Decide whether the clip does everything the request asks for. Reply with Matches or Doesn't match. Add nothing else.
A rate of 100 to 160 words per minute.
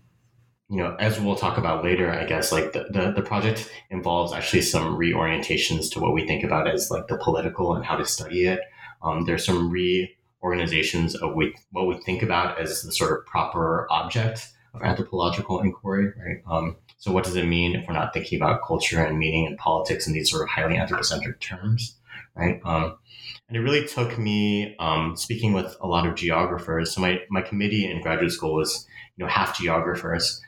Doesn't match